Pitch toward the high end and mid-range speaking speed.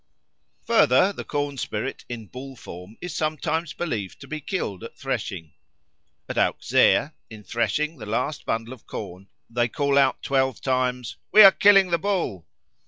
No: low, 130 Hz; average, 160 wpm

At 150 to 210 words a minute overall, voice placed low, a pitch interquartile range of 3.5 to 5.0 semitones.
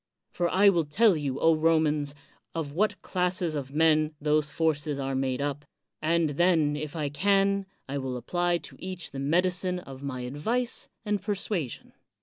No: average, 165 wpm; medium, 155 Hz; average, 4.0 semitones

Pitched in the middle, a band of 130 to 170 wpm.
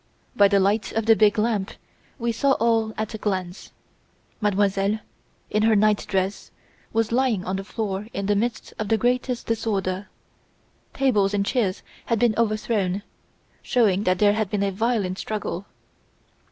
No: high, 210 Hz; average, 160 wpm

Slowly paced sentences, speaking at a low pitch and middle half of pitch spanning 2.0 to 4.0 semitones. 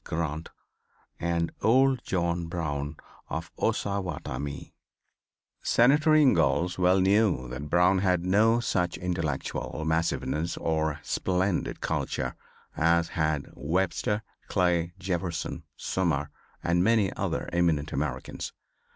Yes: slow, 100 wpm; very low, 85 Hz; average, 3.1 semitones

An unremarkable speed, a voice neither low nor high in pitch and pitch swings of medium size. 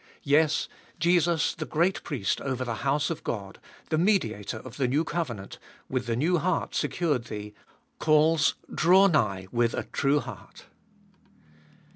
No: average, 145 wpm; medium, 145 Hz; wide, 5.8 semitones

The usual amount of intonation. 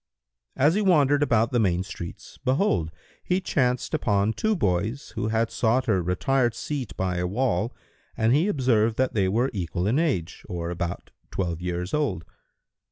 No: wide, 6.7 semitones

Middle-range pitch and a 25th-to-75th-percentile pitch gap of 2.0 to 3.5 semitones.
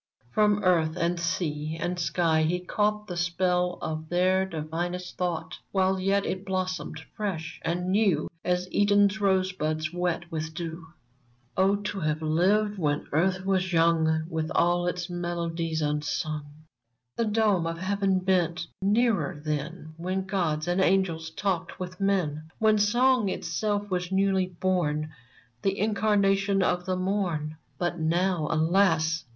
Yes: medium, 180 Hz; average, 3.1 semitones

